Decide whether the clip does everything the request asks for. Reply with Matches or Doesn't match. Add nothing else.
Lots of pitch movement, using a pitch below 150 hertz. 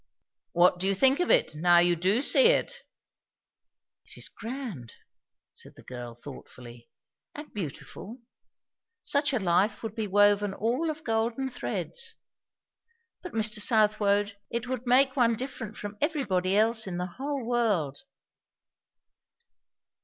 Doesn't match